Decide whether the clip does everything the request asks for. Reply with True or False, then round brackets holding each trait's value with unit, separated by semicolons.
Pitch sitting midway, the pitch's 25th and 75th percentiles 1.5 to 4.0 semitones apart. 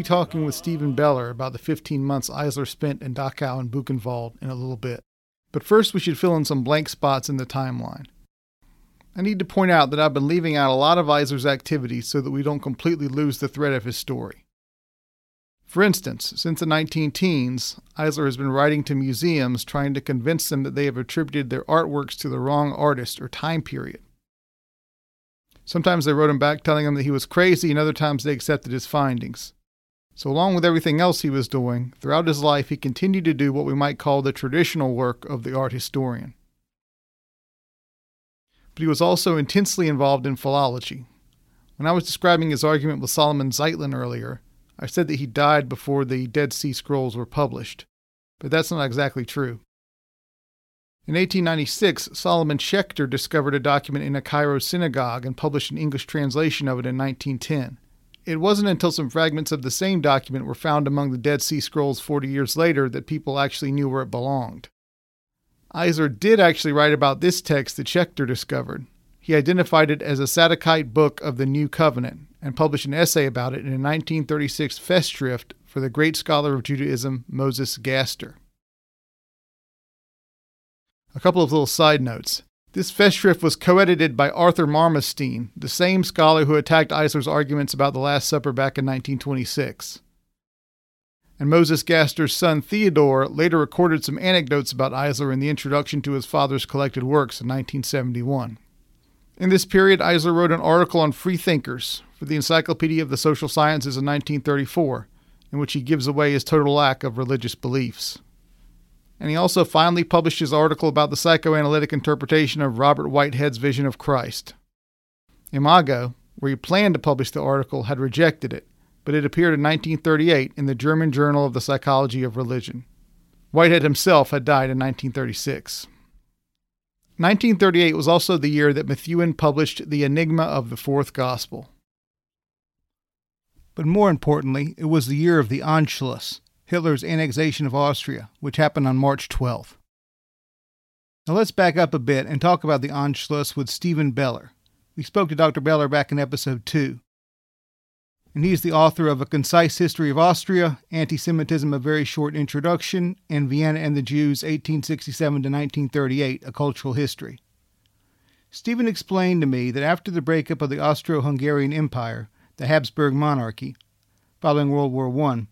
True (145 Hz; 2.9 semitones)